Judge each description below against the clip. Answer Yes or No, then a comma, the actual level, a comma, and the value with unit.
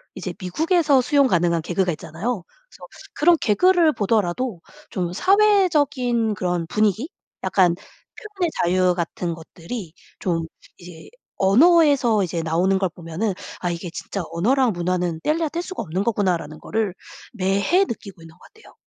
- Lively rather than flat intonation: Yes, wide, 8.1 semitones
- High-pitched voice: Yes, high, 195 Hz